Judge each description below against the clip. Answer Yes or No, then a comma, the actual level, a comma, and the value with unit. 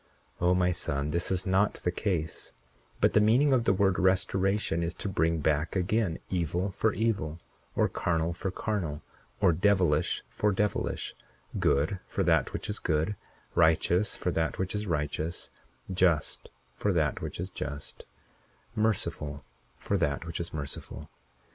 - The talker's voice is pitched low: Yes, very low, 90 Hz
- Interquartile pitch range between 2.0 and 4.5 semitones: Yes, average, 3.8 semitones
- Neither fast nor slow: Yes, average, 155 wpm